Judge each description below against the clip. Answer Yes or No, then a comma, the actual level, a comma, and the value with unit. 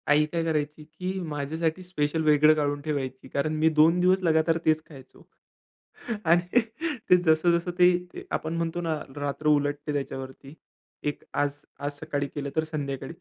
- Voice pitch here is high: No, medium, 155 Hz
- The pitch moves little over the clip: Yes, narrow, 2.3 semitones